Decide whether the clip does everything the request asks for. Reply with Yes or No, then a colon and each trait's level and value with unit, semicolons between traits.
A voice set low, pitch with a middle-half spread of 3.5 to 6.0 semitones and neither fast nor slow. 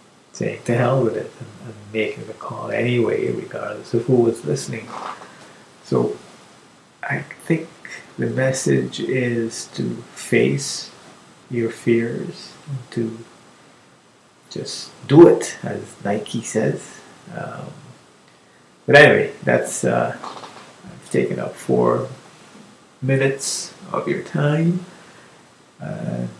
No: low, 120 Hz; average, 4.8 semitones; slow, 105 wpm